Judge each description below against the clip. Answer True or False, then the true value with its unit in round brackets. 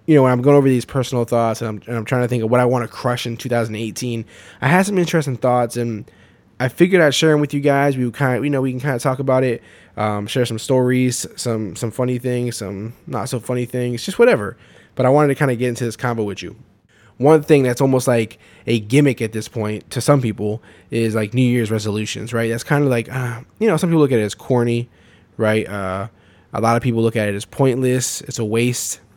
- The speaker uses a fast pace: True (255 wpm)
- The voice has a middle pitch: False (120 Hz)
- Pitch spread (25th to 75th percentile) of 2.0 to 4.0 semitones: True (2.9 semitones)